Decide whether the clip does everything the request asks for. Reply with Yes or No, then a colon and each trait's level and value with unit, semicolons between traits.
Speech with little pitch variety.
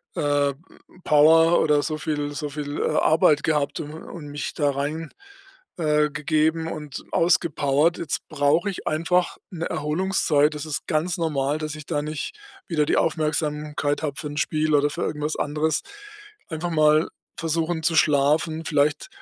Yes: narrow, 1.6 semitones